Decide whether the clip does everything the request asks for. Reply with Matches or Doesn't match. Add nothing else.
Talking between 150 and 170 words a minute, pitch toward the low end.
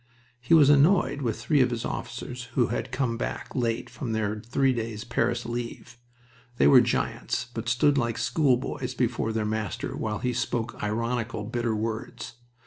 Matches